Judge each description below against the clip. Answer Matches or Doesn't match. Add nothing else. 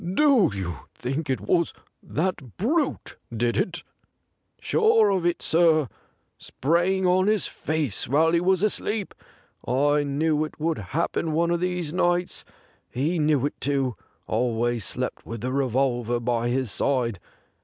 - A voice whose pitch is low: Doesn't match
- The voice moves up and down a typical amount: Doesn't match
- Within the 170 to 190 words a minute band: Doesn't match